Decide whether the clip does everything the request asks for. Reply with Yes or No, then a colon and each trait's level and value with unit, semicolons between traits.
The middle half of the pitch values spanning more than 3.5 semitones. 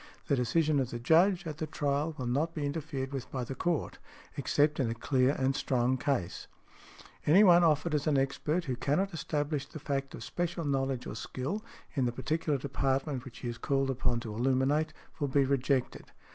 No: average, 2.9 semitones